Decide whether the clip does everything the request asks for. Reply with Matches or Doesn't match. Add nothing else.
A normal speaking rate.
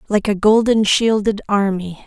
Matches